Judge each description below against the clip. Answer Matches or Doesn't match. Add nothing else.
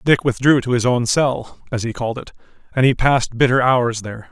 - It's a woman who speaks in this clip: Doesn't match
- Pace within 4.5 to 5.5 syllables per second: Doesn't match